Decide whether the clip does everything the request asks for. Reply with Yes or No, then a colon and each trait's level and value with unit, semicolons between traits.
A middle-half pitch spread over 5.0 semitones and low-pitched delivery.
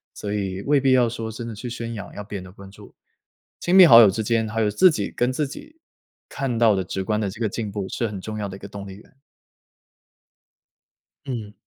No: average, 3.2 semitones; low, 110 Hz